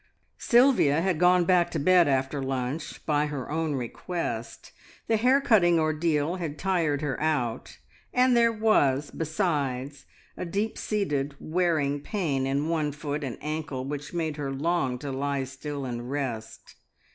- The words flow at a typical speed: Yes, average, 150 wpm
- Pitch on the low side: No, medium, 150 Hz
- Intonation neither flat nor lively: Yes, average, 4.1 semitones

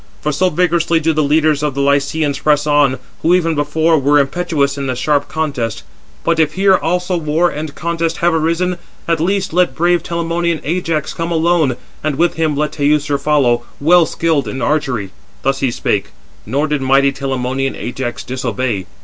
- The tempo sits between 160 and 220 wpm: Yes, average, 175 wpm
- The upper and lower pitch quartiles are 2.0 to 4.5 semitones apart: Yes, average, 3.2 semitones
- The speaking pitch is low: No, medium, 150 Hz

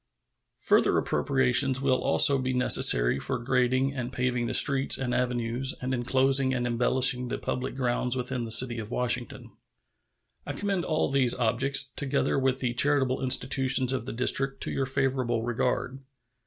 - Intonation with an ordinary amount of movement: No, narrow, 1.6 semitones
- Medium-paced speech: Yes, average, 155 wpm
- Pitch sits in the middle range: No, low, 130 Hz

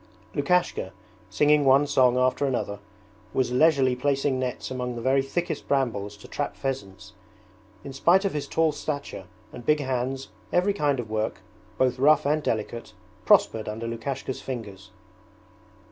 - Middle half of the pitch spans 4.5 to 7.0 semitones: No, average, 3.4 semitones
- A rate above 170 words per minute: No, average, 145 wpm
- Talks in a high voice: No, low, 130 Hz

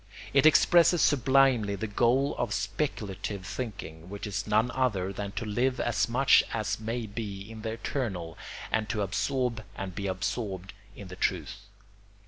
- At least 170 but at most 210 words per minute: No, average, 155 wpm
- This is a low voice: Yes, low, 110 Hz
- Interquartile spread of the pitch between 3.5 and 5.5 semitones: Yes, average, 4.1 semitones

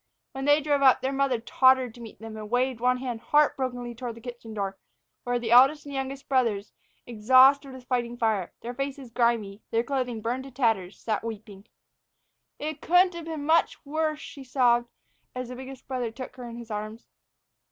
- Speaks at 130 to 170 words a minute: No, average, 195 wpm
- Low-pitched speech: No, very high, 250 Hz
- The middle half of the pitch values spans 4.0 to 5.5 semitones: No, average, 2.9 semitones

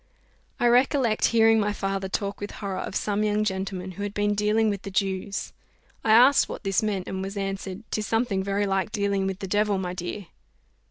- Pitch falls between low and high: No, high, 200 Hz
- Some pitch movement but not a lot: No, narrow, 1.7 semitones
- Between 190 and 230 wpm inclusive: Yes, fast, 205 wpm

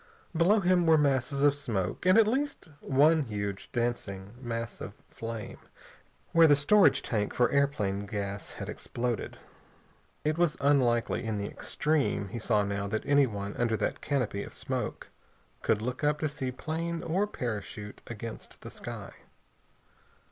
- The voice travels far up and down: Yes, wide, 6.4 semitones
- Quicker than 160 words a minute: No, average, 150 wpm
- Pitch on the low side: Yes, low, 125 Hz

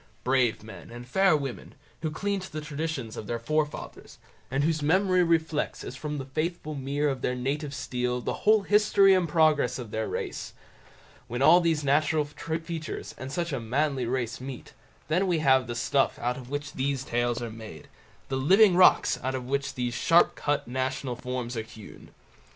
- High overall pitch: No, medium, 140 Hz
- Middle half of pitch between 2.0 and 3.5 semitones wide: No, average, 4.2 semitones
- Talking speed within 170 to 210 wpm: Yes, average, 185 wpm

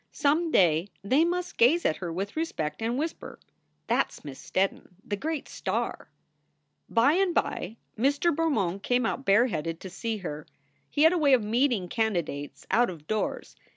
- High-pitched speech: Yes, high, 225 Hz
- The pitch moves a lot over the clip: Yes, wide, 8.1 semitones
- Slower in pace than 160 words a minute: No, average, 170 wpm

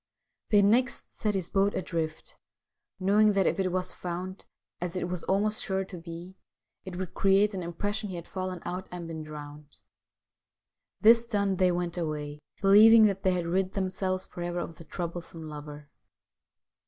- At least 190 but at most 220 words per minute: No, average, 175 wpm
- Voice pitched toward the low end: No, medium, 185 Hz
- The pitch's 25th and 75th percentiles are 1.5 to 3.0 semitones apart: Yes, narrow, 2.5 semitones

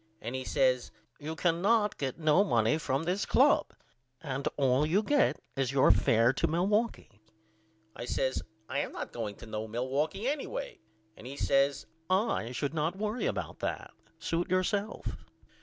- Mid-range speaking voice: Yes, medium, 145 Hz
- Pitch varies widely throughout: Yes, wide, 6.8 semitones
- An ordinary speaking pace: Yes, average, 155 wpm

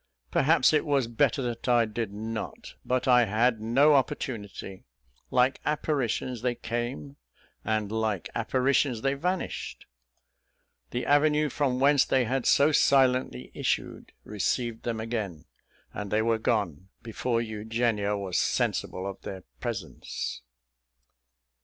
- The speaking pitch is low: Yes, low, 120 Hz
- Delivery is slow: Yes, slow, 125 wpm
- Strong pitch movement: No, average, 3.6 semitones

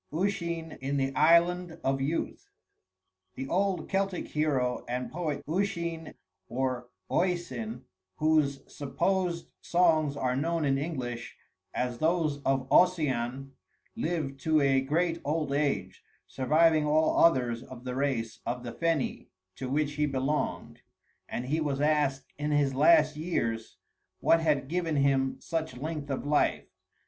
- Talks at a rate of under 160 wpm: Yes, slow, 135 wpm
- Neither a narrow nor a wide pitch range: Yes, average, 3.7 semitones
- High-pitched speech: No, medium, 150 Hz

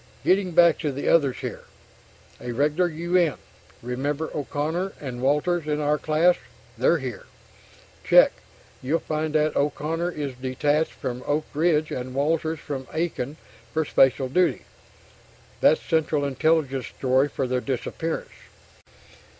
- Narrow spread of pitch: No, average, 3.3 semitones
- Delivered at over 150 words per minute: No, slow, 135 wpm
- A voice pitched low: No, medium, 150 Hz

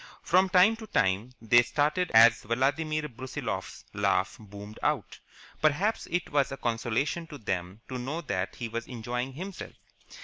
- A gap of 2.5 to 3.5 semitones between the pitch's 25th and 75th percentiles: No, average, 5.3 semitones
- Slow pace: No, average, 150 wpm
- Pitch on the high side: No, low, 130 Hz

